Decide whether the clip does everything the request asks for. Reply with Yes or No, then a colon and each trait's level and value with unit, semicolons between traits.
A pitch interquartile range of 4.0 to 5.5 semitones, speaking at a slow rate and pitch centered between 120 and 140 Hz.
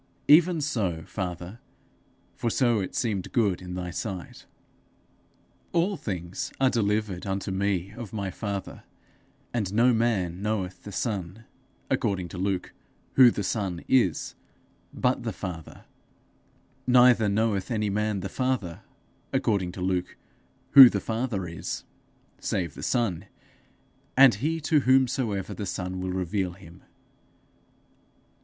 No: average, 4.4 semitones; slow, 130 wpm; low, 100 Hz